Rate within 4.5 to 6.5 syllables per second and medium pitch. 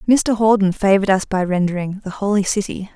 No: 5.9 syllables/s; high, 200 Hz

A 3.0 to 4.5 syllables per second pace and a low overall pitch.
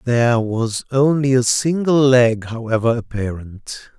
Yes: 4.2 syllables/s; low, 120 Hz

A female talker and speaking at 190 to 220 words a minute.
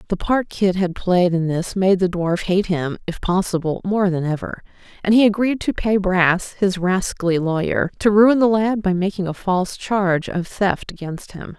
Yes: female; average, 200 wpm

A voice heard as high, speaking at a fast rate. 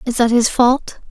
Yes: high, 245 Hz; fast, 220 wpm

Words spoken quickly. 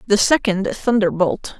No: slow, 115 wpm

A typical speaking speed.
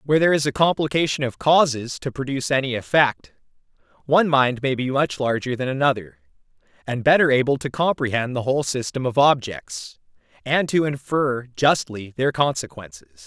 Yes: average, 160 wpm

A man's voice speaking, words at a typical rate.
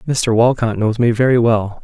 Yes: male; average, 195 wpm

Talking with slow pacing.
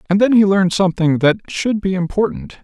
No: fast, 205 wpm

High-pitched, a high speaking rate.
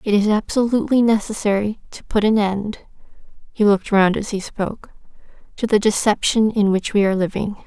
No: high, 210 Hz; average, 155 wpm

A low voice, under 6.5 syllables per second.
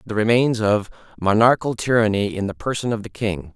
Yes: low, 110 Hz; 5.8 syllables/s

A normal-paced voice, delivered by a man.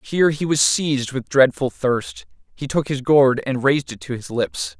No: fast, 215 wpm; male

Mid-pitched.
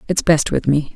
Yes: medium, 150 Hz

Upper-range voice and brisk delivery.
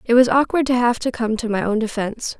Yes: high, 235 Hz; fast, 275 wpm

